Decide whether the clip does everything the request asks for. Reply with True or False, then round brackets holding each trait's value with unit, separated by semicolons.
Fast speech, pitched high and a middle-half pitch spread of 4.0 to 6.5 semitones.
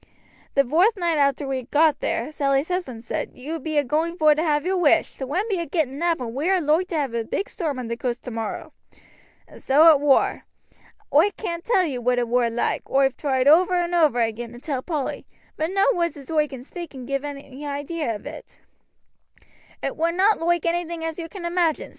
True (220 wpm; 300 Hz; 4.3 semitones)